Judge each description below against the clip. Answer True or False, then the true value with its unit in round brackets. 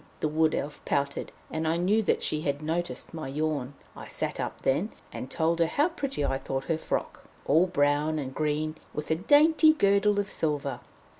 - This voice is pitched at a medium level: True (155 Hz)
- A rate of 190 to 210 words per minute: True (195 wpm)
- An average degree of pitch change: True (4.2 semitones)